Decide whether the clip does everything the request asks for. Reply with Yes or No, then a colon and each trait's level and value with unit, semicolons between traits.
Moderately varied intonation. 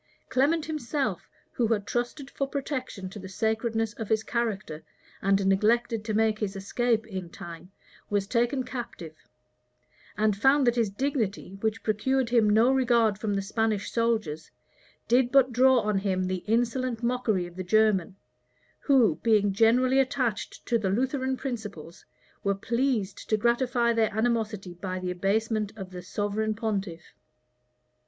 Yes: average, 3.6 semitones